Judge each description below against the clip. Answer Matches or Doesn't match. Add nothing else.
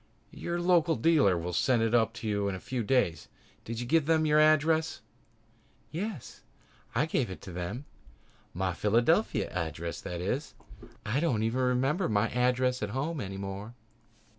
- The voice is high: Doesn't match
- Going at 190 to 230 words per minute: Doesn't match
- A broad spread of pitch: Matches